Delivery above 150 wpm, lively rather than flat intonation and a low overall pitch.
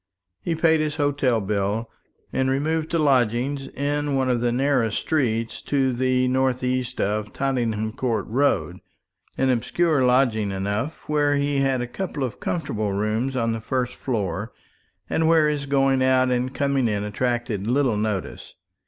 No: average, 160 wpm; average, 3.8 semitones; low, 130 Hz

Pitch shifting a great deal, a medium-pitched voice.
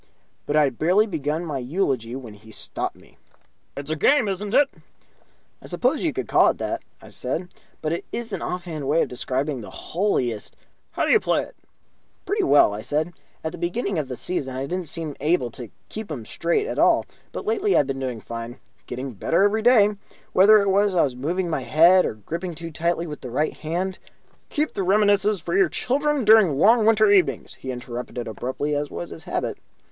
Yes: wide, 7.0 semitones; medium, 165 Hz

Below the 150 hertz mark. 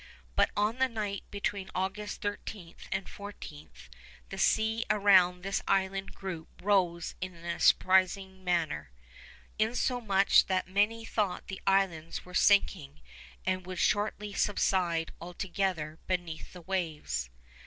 No: high, 190 Hz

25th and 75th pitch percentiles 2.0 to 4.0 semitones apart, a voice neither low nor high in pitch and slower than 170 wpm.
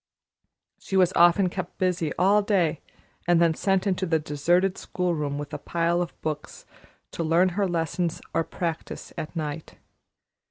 Yes: narrow, 2.4 semitones; medium, 170 Hz; average, 160 wpm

